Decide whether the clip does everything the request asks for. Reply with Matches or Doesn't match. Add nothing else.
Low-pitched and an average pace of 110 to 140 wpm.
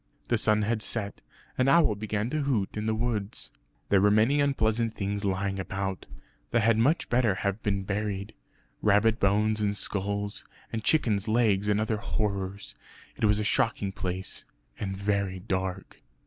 Doesn't match